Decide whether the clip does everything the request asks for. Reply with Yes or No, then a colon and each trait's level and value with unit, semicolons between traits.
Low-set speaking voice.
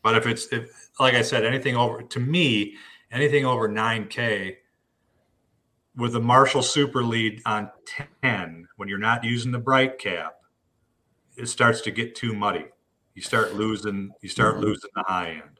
Yes: low, 115 Hz